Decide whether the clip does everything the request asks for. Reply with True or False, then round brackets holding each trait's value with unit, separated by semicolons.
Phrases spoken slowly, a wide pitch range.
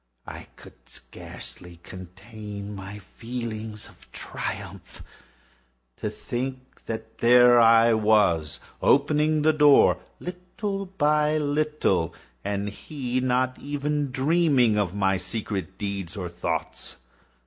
True (110 wpm; 6.5 semitones)